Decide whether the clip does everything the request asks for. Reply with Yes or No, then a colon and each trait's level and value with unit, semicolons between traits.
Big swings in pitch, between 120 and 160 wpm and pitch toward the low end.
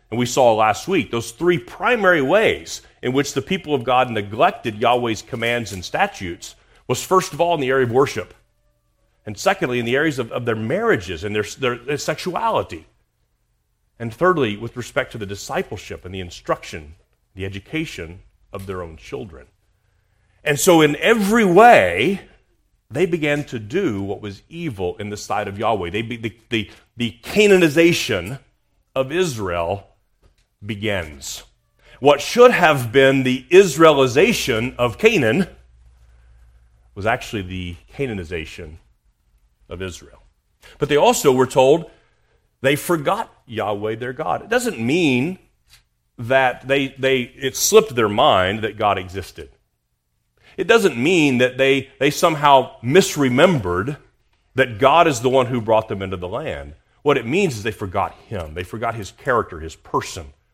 Yes: wide, 5.9 semitones; average, 155 wpm; low, 120 Hz